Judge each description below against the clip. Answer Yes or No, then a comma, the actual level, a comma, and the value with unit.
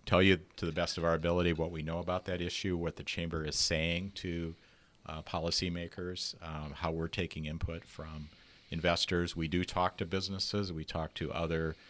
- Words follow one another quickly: No, average, 190 wpm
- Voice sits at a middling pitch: No, very low, 85 Hz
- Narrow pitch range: Yes, narrow, 1.8 semitones